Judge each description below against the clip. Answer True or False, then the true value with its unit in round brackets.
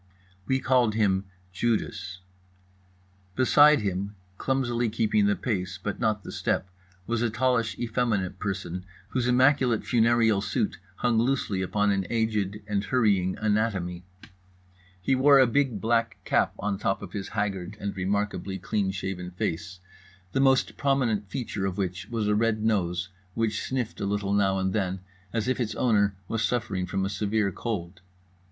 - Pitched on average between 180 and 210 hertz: False (105 Hz)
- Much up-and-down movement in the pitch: False (3.4 semitones)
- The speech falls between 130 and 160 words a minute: True (155 wpm)